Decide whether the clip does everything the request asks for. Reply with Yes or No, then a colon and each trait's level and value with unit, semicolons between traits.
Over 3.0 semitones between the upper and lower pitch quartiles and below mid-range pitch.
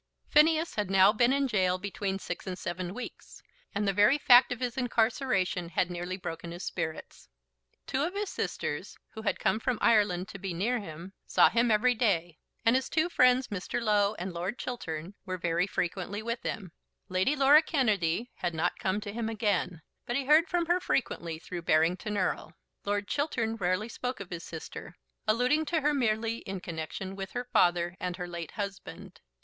No: wide, 5.5 semitones; high, 205 Hz